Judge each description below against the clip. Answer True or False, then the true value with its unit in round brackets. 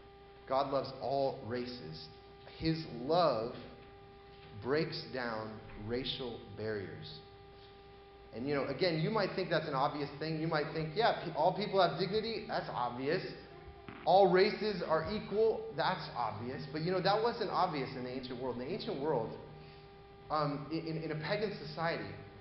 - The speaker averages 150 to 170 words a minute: True (155 wpm)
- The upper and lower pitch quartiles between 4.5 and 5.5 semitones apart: True (4.8 semitones)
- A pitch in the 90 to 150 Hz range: True (135 Hz)